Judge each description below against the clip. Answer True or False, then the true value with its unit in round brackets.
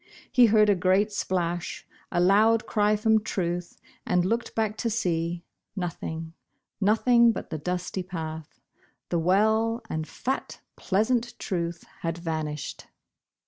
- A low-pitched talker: False (185 Hz)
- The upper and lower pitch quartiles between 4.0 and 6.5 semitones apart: True (4.4 semitones)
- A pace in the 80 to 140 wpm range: True (135 wpm)